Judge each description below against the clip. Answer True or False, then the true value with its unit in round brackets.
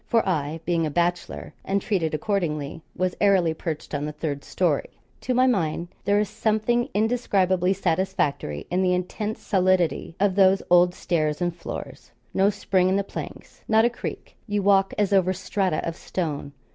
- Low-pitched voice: False (185 Hz)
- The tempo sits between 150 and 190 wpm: True (170 wpm)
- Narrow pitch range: False (3.5 semitones)